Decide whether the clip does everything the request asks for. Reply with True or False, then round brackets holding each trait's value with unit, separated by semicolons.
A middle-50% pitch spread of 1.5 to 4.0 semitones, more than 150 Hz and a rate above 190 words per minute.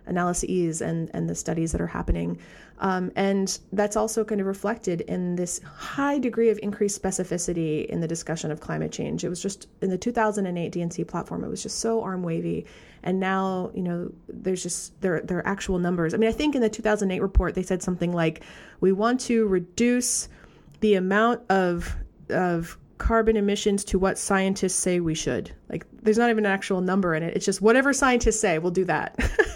True (3.6 semitones; 190 Hz; 200 wpm)